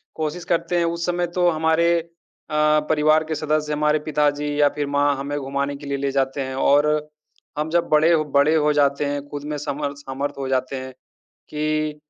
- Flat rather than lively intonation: Yes, narrow, 1.5 semitones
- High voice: No, medium, 150 Hz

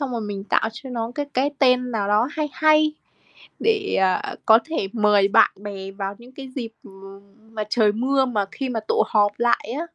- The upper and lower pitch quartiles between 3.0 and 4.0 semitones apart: No, average, 4.4 semitones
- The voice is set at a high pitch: Yes, high, 235 Hz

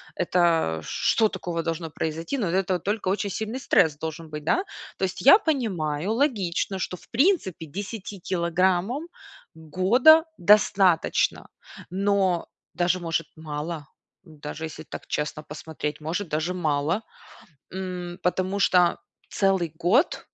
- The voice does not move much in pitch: No, average, 3.8 semitones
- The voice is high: No, medium, 180 Hz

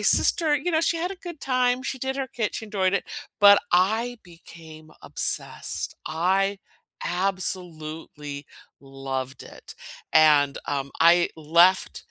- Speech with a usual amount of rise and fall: No, wide, 7.7 semitones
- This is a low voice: No, medium, 185 Hz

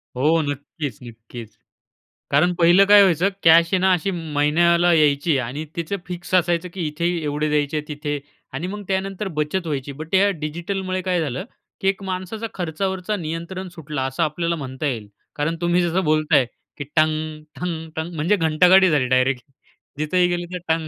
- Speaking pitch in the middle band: Yes, medium, 165 Hz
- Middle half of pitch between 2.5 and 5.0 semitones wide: Yes, average, 3.4 semitones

